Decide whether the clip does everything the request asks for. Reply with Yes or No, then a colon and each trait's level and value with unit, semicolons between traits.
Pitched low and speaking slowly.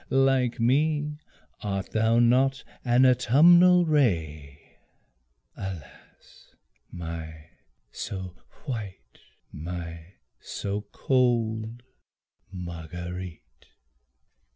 Yes: low, 110 Hz; slow, 65 wpm